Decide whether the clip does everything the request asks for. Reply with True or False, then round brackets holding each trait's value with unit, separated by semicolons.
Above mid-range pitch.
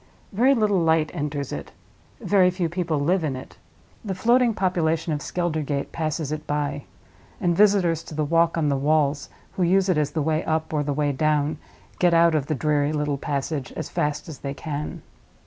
False (155 Hz)